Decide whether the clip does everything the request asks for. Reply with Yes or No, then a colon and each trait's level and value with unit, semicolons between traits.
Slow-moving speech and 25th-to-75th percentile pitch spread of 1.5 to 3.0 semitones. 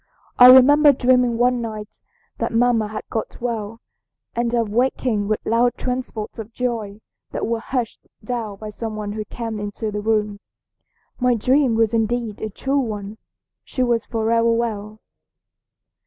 No: average, 155 wpm; narrow, 2.4 semitones